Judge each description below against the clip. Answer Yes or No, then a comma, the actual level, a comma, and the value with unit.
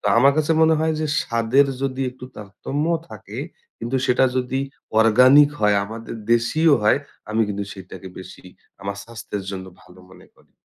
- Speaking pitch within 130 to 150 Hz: No, low, 120 Hz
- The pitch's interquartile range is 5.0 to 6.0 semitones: Yes, average, 5.3 semitones